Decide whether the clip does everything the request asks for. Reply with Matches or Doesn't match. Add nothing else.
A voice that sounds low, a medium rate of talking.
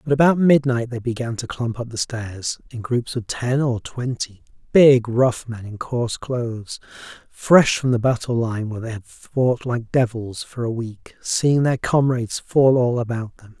Matches